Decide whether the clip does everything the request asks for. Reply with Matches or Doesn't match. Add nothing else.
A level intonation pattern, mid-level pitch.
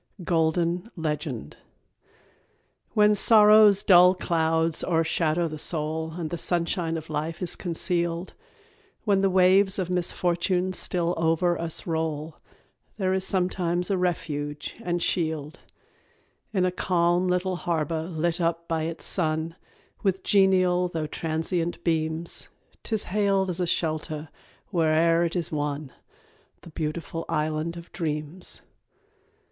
Matches